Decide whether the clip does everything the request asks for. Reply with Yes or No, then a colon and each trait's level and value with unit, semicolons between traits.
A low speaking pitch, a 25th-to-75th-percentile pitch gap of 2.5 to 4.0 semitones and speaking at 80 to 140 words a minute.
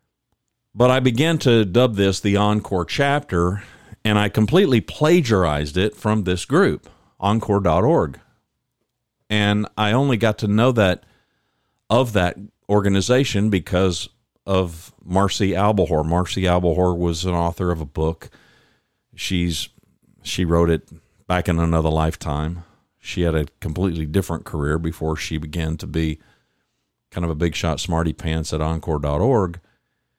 No: very low, 95 Hz; average, 4.4 semitones; slow, 135 wpm